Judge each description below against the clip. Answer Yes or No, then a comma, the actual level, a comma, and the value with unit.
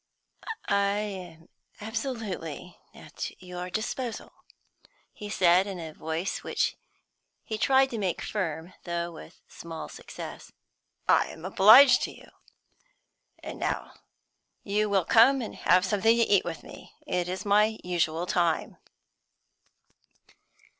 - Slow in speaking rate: Yes, slow, 125 wpm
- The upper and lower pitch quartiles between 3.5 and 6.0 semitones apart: Yes, average, 3.9 semitones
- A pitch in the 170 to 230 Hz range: Yes, high, 190 Hz